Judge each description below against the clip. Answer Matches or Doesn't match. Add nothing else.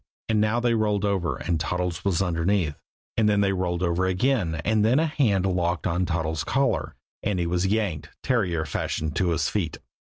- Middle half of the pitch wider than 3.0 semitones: Matches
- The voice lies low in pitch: Matches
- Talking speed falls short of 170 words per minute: Doesn't match